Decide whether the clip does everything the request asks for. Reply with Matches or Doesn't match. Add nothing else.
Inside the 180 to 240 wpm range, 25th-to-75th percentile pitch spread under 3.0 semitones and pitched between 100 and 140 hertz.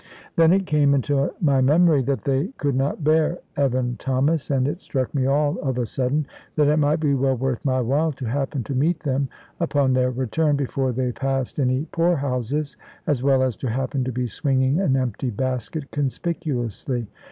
Matches